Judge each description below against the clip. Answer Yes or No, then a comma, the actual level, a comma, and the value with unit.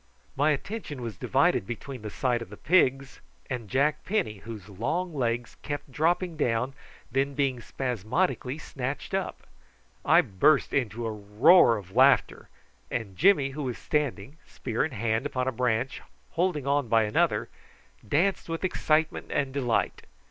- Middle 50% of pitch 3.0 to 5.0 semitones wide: Yes, average, 4.7 semitones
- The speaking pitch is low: Yes, low, 130 Hz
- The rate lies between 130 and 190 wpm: Yes, average, 155 wpm